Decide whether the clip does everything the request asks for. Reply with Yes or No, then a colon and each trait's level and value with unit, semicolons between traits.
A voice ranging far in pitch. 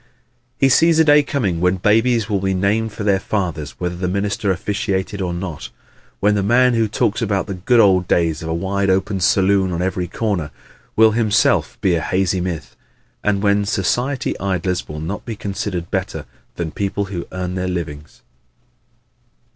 No: narrow, 2.6 semitones